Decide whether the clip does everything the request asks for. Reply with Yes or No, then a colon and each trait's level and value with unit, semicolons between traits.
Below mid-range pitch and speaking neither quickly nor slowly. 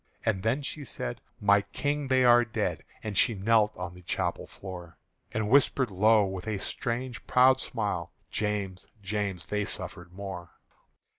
Yes: low, 105 Hz; average, 155 wpm